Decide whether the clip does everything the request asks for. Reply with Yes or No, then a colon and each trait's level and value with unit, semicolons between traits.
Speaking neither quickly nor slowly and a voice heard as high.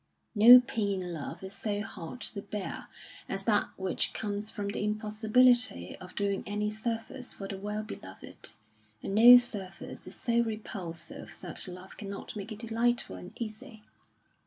Yes: average, 160 wpm; high, 210 Hz